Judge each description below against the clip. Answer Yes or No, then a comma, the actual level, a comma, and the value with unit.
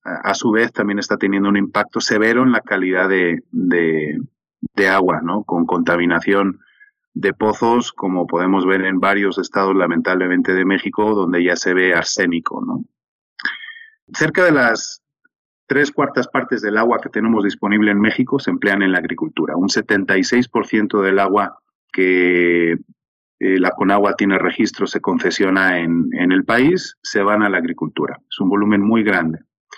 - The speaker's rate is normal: Yes, average, 160 wpm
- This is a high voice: No, low, 100 Hz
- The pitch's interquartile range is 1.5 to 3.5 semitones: Yes, average, 3.2 semitones